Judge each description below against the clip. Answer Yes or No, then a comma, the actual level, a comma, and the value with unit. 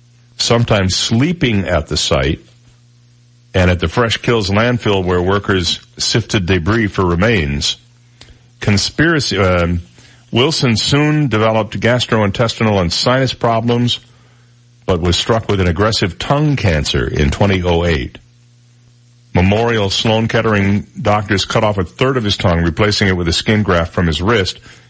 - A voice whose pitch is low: Yes, low, 110 Hz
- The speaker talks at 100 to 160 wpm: Yes, slow, 135 wpm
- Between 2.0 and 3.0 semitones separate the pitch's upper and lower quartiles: No, average, 4.4 semitones